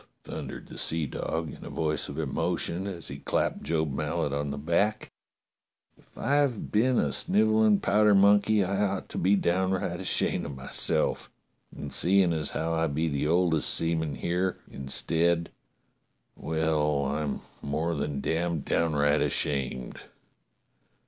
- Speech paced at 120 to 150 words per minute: Yes, average, 140 wpm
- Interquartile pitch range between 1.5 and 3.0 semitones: No, average, 4.6 semitones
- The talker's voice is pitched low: Yes, very low, 80 Hz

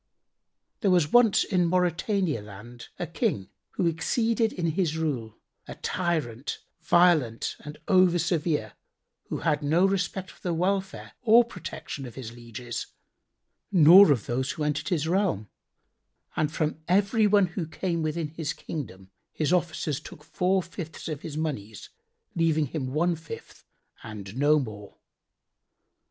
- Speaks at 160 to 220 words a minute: No, average, 140 wpm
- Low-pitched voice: No, medium, 160 Hz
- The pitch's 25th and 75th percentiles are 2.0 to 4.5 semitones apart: No, average, 4.9 semitones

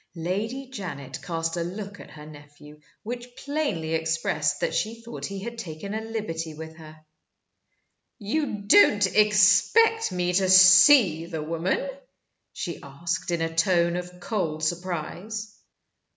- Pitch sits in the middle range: Yes, medium, 180 Hz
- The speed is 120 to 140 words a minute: Yes, slow, 135 wpm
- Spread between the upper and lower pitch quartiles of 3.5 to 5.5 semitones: Yes, average, 4.7 semitones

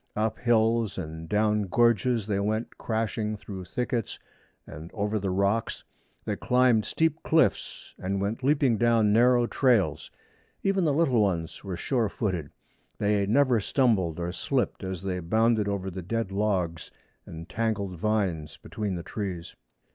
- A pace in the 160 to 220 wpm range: No, average, 145 wpm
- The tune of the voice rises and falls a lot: No, average, 3.8 semitones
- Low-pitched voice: Yes, low, 105 Hz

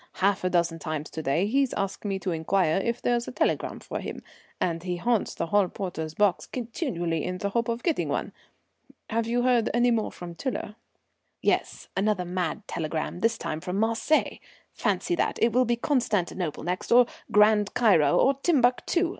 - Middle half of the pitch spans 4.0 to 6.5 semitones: Yes, average, 5.3 semitones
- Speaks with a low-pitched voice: No, high, 205 Hz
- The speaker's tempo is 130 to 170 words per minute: No, average, 180 wpm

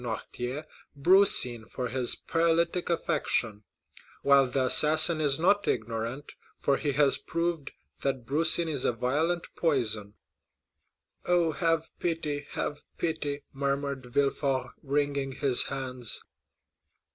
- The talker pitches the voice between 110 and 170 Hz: Yes, medium, 140 Hz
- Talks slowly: Yes, slow, 110 wpm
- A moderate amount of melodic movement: Yes, average, 4.1 semitones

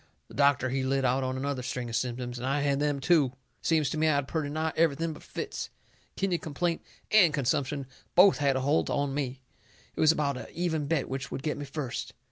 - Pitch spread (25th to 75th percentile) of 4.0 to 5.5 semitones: No, average, 3.0 semitones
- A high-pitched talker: No, medium, 140 Hz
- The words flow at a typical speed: No, fast, 225 wpm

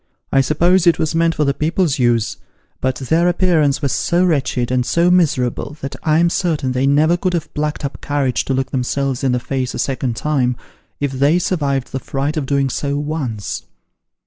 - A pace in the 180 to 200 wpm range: Yes, average, 195 wpm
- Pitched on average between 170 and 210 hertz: No, medium, 140 Hz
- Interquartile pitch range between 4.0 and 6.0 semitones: No, average, 3.6 semitones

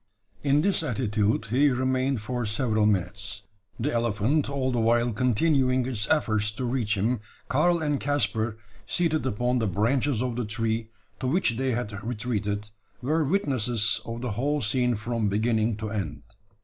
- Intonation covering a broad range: No, average, 3.5 semitones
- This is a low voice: Yes, low, 120 Hz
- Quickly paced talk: No, average, 160 wpm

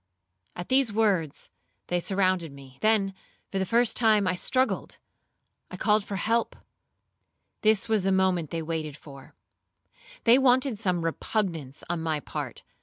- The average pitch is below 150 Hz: No, high, 190 Hz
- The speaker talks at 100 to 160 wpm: Yes, slow, 135 wpm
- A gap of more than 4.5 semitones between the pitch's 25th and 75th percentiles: Yes, average, 4.9 semitones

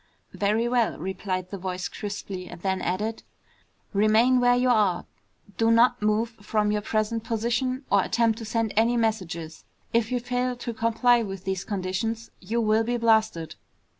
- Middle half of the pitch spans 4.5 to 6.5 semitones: No, average, 3.2 semitones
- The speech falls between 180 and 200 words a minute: No, average, 165 wpm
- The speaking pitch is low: No, high, 220 Hz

